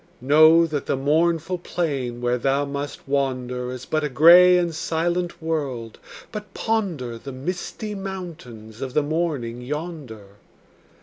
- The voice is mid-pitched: Yes, medium, 150 Hz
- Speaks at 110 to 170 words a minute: Yes, slow, 135 wpm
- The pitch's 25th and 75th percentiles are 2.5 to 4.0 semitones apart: No, average, 5.2 semitones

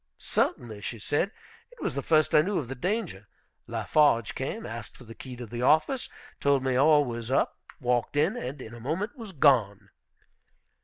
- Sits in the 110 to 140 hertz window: Yes, low, 135 Hz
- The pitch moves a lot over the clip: No, average, 4.8 semitones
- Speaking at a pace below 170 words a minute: No, average, 190 wpm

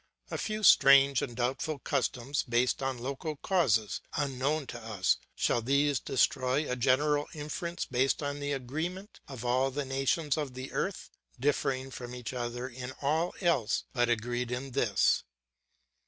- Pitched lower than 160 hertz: Yes, low, 135 Hz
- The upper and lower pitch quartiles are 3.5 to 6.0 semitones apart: No, average, 2.9 semitones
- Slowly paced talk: No, average, 155 wpm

